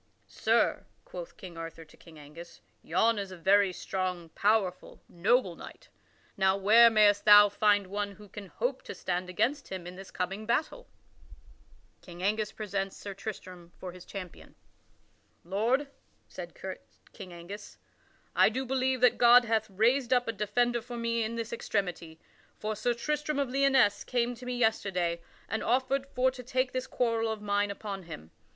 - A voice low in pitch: No, high, 210 Hz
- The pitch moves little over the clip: No, average, 4.5 semitones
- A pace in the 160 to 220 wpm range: Yes, average, 170 wpm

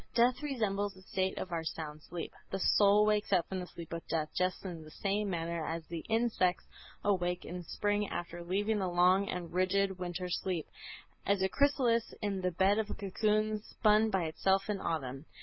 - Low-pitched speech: No, high, 190 Hz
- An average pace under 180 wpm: No, average, 195 wpm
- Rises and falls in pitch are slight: No, average, 3.1 semitones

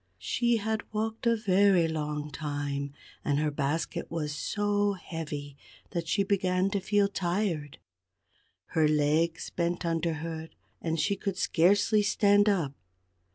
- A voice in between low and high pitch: Yes, medium, 170 Hz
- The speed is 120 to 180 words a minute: Yes, slow, 135 wpm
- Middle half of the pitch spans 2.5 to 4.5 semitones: No, average, 4.9 semitones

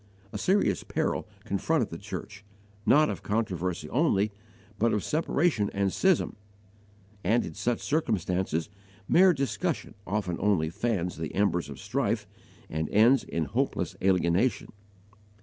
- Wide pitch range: Yes, wide, 6.2 semitones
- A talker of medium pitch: No, low, 105 Hz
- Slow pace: Yes, slow, 130 wpm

